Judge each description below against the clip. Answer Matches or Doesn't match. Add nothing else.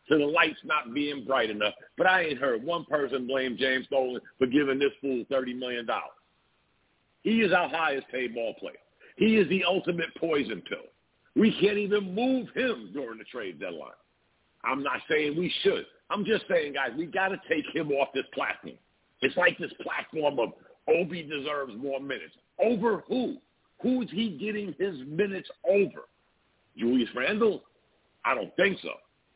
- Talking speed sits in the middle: Matches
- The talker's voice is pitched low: Doesn't match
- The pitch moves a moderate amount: Doesn't match